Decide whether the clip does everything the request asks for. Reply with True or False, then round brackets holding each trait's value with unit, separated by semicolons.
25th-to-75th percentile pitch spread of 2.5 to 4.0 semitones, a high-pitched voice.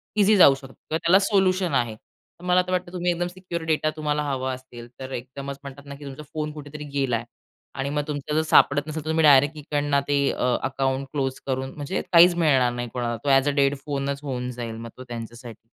False (3.0 semitones; 140 Hz)